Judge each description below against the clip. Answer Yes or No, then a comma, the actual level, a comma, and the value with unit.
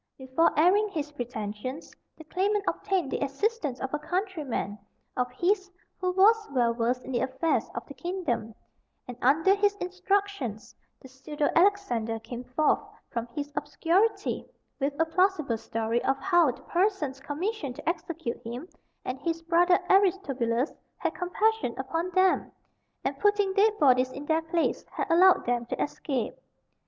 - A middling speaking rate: Yes, average, 150 wpm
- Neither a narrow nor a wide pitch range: No, wide, 6.8 semitones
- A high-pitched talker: Yes, very high, 310 Hz